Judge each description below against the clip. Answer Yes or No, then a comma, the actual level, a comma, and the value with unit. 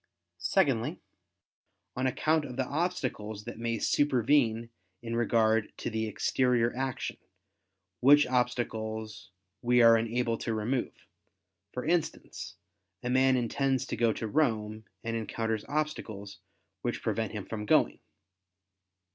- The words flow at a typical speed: No, slow, 120 wpm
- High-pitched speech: No, low, 115 Hz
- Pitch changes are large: No, average, 3.0 semitones